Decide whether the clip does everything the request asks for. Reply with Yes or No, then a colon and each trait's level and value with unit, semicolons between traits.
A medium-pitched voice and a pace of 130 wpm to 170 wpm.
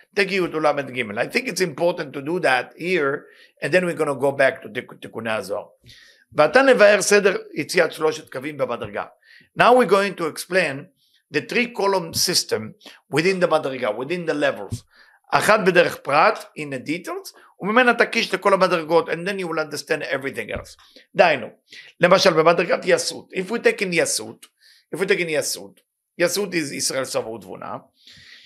Yes: medium, 180 Hz; slow, 135 wpm